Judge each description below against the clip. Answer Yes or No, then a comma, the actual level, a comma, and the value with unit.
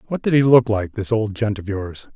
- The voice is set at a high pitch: No, low, 110 Hz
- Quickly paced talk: Yes, fast, 250 wpm